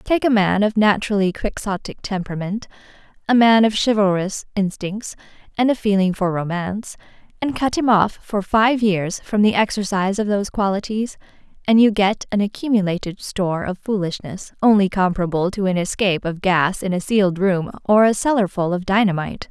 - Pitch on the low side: No, high, 200 Hz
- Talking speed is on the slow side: No, average, 165 wpm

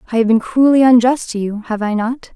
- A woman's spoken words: Yes, female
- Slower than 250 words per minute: No, fast, 255 wpm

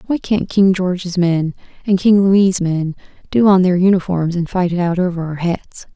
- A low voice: No, medium, 180 Hz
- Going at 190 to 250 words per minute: Yes, average, 200 wpm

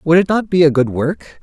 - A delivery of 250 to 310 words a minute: Yes, fast, 295 wpm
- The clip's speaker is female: No, male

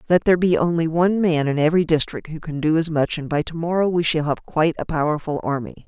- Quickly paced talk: Yes, fast, 255 wpm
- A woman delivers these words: Yes, female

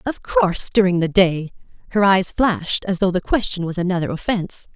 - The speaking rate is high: No, average, 190 wpm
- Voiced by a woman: Yes, female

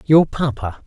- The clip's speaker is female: No, male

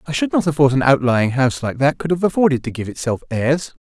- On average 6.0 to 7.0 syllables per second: Yes, 6.1 syllables/s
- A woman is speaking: No, male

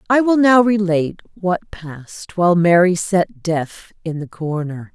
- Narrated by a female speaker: Yes, female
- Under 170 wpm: Yes, average, 160 wpm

